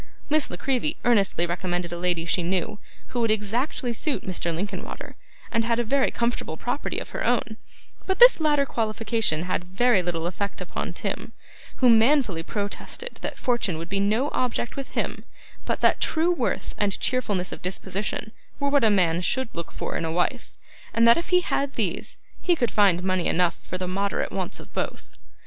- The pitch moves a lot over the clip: Yes, wide, 5.8 semitones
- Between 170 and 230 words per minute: Yes, average, 190 wpm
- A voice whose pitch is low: No, high, 215 Hz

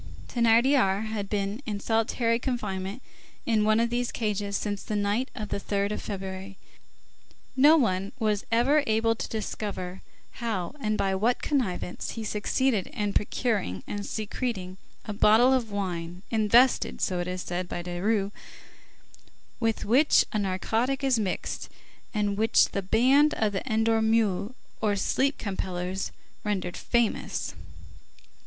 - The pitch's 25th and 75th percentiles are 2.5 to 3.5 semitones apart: Yes, average, 3.0 semitones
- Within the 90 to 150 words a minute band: Yes, average, 140 wpm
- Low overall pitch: No, high, 210 Hz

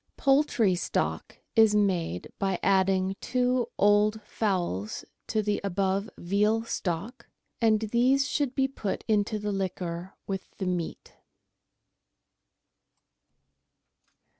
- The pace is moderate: No, slow, 105 wpm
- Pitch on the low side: No, high, 205 Hz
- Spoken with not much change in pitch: No, average, 3.1 semitones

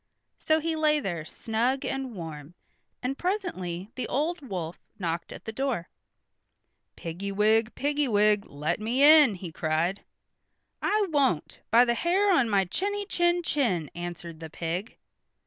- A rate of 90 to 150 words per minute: Yes, average, 145 wpm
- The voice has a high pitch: Yes, high, 225 Hz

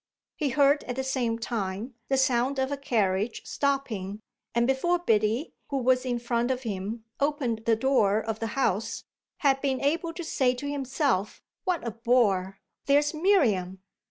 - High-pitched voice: Yes, very high, 250 Hz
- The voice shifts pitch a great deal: No, average, 3.9 semitones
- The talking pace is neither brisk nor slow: Yes, average, 165 wpm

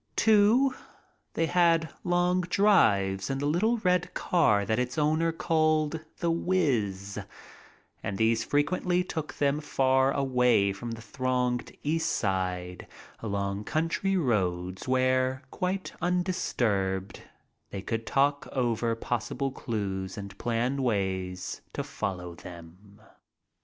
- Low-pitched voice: Yes, low, 130 Hz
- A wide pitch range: Yes, wide, 8.5 semitones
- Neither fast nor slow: No, slow, 115 wpm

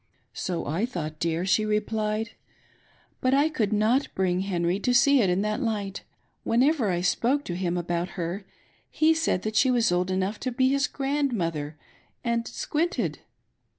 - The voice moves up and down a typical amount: No, wide, 6.1 semitones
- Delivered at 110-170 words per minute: No, average, 180 wpm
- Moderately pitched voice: No, high, 215 Hz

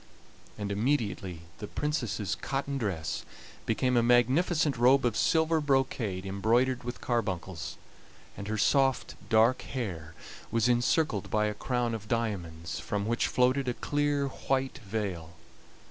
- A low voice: Yes, low, 120 Hz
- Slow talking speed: Yes, slow, 130 wpm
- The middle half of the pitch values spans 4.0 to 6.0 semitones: Yes, average, 4.7 semitones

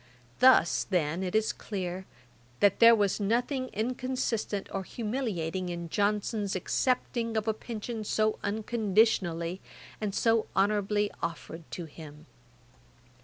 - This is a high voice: Yes, high, 205 Hz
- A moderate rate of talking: No, slow, 120 wpm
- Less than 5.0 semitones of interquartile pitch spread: Yes, average, 3.7 semitones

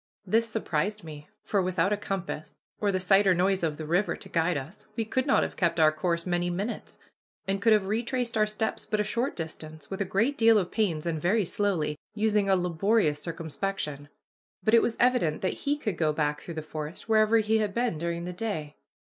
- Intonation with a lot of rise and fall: No, average, 4.8 semitones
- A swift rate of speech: Yes, fast, 215 wpm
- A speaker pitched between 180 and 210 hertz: Yes, high, 190 Hz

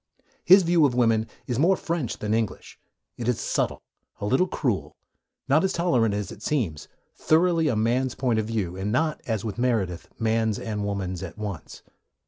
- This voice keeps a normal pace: Yes, average, 180 wpm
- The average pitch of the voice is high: No, low, 115 Hz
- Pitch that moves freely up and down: Yes, wide, 6.0 semitones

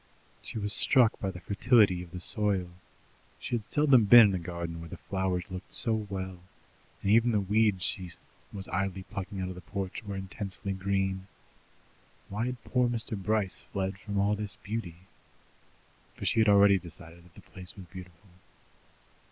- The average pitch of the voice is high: No, low, 100 Hz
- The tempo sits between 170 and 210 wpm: Yes, average, 175 wpm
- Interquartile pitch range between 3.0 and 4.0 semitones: No, narrow, 2.5 semitones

